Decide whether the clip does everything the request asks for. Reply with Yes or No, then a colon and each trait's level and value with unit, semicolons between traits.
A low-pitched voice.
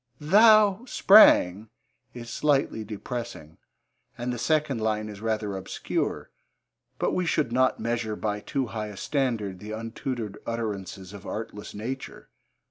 Yes: low, 115 Hz